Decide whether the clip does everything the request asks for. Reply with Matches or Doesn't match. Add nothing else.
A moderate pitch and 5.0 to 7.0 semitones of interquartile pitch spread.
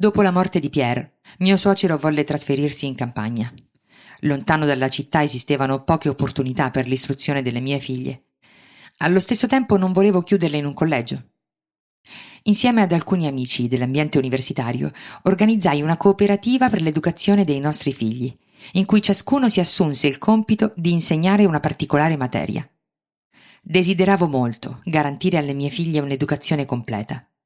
Matches